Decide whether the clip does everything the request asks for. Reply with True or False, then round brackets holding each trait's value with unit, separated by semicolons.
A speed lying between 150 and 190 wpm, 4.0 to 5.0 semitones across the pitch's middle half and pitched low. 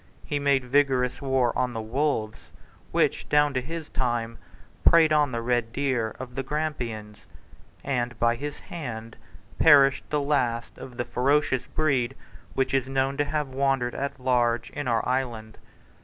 False (155 wpm; 3.0 semitones; 130 Hz)